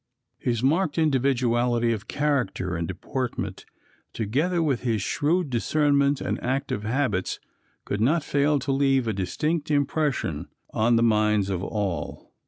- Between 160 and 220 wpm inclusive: No, slow, 135 wpm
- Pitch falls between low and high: No, low, 125 Hz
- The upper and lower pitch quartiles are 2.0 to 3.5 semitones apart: No, average, 5.1 semitones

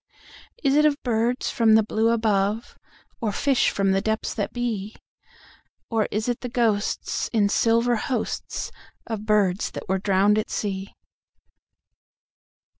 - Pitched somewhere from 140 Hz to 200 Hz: No, high, 220 Hz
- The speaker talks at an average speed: No, slow, 120 wpm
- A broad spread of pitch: No, narrow, 2.5 semitones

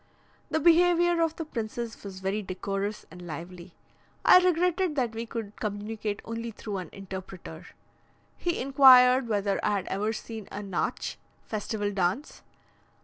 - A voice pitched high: Yes, high, 215 Hz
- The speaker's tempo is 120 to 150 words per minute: Yes, average, 145 wpm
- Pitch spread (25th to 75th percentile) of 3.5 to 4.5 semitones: No, wide, 5.4 semitones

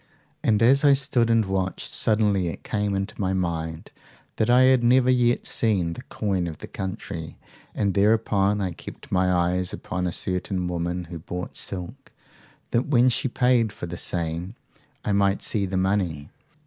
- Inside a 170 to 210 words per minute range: Yes, average, 175 wpm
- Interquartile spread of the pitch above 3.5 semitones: Yes, average, 4.3 semitones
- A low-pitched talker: Yes, very low, 95 Hz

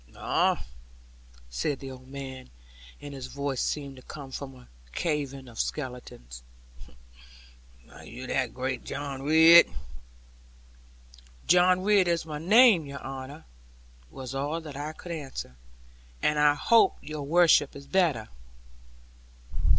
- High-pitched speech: No, medium, 140 Hz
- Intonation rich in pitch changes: No, average, 3.3 semitones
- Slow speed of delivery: Yes, slow, 125 wpm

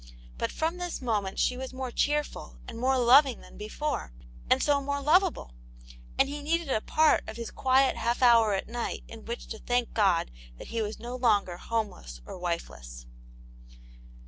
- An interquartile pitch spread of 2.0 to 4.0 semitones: No, average, 4.8 semitones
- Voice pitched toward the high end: Yes, high, 240 Hz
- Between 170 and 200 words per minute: Yes, average, 175 wpm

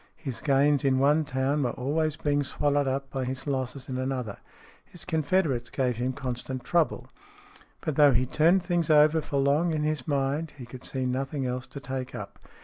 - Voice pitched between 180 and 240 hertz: No, medium, 140 Hz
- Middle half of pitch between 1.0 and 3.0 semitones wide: Yes, narrow, 2.6 semitones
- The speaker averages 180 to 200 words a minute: Yes, average, 190 wpm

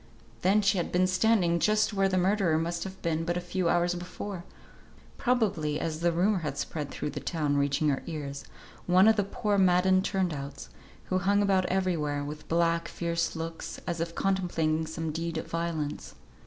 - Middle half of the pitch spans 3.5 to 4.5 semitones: No, average, 2.9 semitones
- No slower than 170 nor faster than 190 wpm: Yes, average, 185 wpm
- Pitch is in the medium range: Yes, medium, 170 Hz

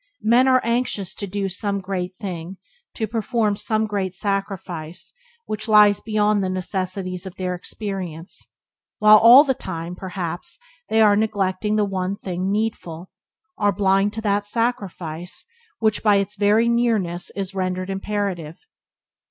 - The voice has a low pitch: No, high, 200 Hz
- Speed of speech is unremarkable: Yes, average, 145 wpm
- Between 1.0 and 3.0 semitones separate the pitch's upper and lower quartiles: Yes, narrow, 2.6 semitones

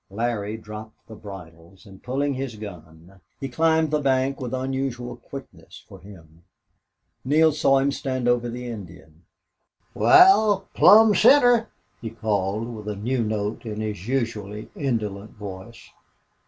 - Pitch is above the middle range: No, low, 115 Hz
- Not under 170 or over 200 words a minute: No, average, 140 wpm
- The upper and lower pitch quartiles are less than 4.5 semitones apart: No, average, 4.9 semitones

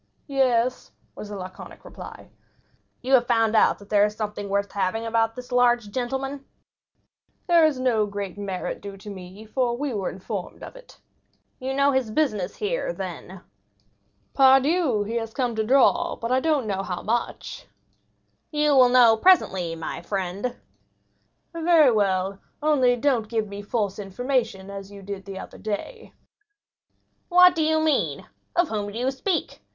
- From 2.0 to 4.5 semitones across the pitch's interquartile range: No, average, 5.0 semitones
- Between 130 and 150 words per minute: No, average, 160 wpm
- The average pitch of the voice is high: Yes, high, 230 Hz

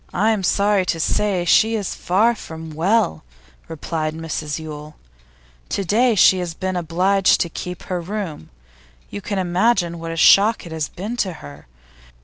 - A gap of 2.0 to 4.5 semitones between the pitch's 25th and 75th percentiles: Yes, average, 3.9 semitones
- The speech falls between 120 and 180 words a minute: Yes, average, 160 wpm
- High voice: No, medium, 180 Hz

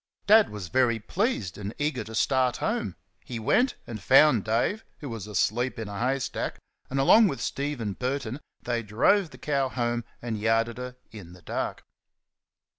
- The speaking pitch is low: Yes, low, 120 Hz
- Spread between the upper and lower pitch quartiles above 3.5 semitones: Yes, average, 3.9 semitones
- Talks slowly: No, average, 175 wpm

